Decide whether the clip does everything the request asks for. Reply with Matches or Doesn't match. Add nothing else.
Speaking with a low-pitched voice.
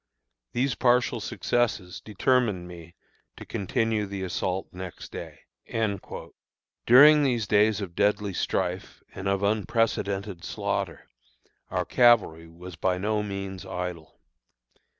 Matches